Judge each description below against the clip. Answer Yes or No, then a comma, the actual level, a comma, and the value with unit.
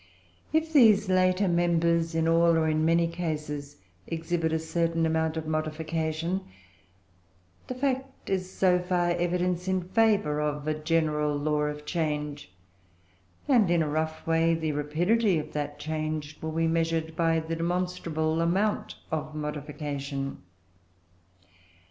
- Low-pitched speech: No, medium, 165 Hz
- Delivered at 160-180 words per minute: No, slow, 135 wpm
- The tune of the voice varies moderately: No, narrow, 2.3 semitones